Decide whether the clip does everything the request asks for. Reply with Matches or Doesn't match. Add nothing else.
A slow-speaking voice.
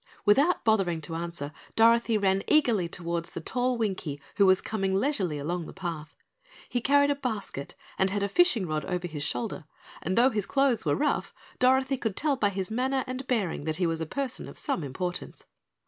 Doesn't match